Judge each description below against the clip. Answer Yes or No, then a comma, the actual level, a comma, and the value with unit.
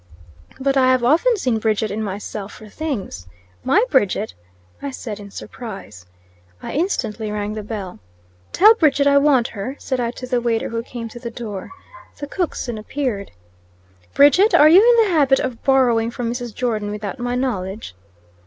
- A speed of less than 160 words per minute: No, average, 175 wpm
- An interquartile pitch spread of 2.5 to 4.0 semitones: No, average, 4.7 semitones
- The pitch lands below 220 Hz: No, high, 240 Hz